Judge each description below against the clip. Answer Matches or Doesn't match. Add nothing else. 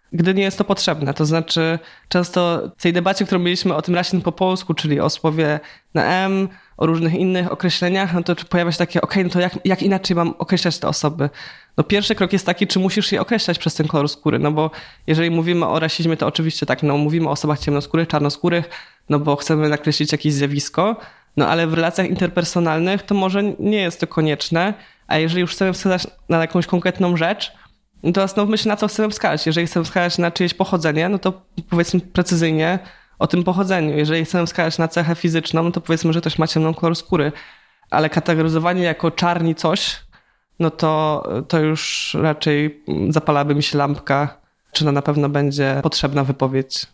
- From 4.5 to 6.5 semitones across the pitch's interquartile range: Doesn't match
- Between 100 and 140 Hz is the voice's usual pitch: Doesn't match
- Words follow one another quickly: Matches